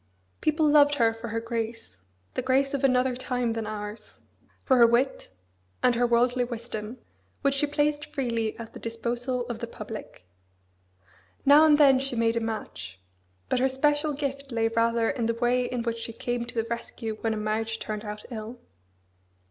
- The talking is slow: No, average, 180 wpm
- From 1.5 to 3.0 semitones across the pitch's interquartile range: Yes, average, 2.7 semitones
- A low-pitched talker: No, high, 235 Hz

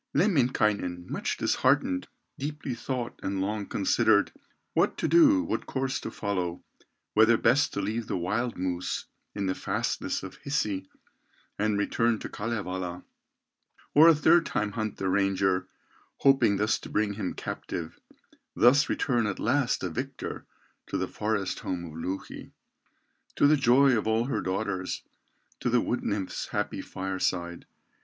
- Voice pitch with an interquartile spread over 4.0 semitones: Yes, average, 4.5 semitones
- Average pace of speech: Yes, average, 150 wpm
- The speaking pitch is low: Yes, low, 105 Hz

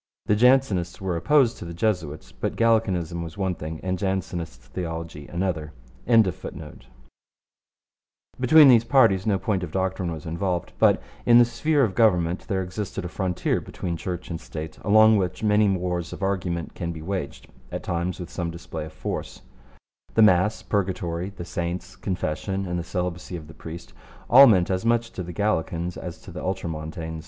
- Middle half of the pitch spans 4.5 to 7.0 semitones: No, average, 3.3 semitones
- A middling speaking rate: Yes, average, 150 wpm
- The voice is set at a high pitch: No, very low, 90 Hz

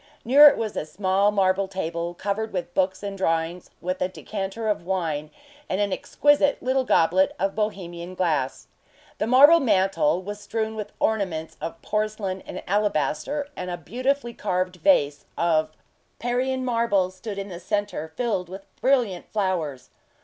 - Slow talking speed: No, average, 155 wpm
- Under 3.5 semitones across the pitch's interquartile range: No, average, 3.9 semitones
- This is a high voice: Yes, high, 195 Hz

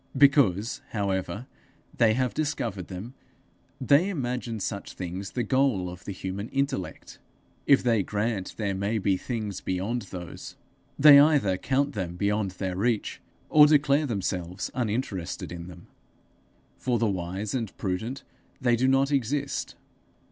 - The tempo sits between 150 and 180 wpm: No, average, 140 wpm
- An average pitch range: No, wide, 5.7 semitones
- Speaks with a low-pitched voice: Yes, low, 110 Hz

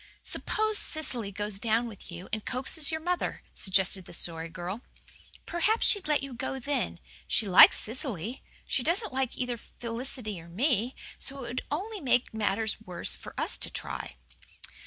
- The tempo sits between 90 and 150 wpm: No, average, 165 wpm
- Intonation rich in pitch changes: Yes, wide, 5.7 semitones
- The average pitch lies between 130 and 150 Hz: No, high, 240 Hz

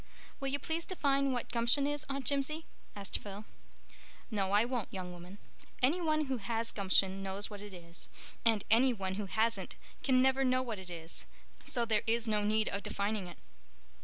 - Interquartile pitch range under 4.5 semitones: No, average, 5.0 semitones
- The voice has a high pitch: Yes, high, 225 Hz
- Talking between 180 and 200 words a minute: Yes, average, 190 wpm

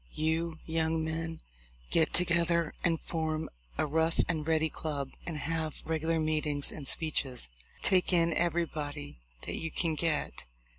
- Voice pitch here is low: No, medium, 160 Hz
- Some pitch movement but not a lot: No, narrow, 1.2 semitones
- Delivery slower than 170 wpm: Yes, average, 140 wpm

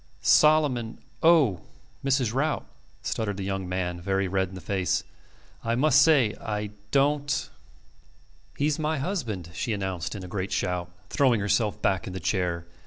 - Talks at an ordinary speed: Yes, average, 160 wpm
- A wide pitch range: Yes, wide, 6.9 semitones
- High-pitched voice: No, low, 105 Hz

